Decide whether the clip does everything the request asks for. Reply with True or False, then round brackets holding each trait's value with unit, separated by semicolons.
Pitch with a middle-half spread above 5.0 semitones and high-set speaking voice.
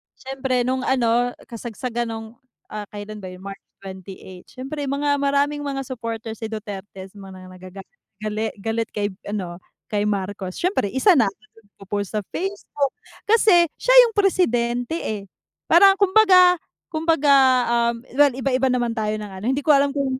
True (5.4 semitones; 240 Hz)